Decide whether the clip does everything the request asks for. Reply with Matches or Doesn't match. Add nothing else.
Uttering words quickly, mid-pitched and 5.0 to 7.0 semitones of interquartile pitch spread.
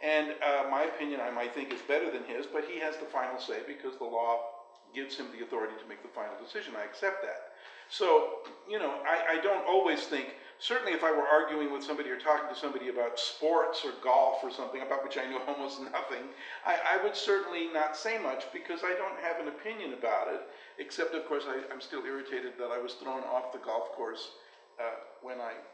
Matches